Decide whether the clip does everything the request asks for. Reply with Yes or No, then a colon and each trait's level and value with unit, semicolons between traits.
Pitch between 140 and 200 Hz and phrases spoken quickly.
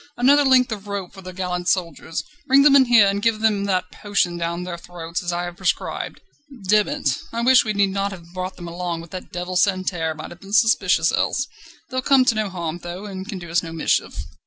Yes: medium, 185 Hz; fast, 230 wpm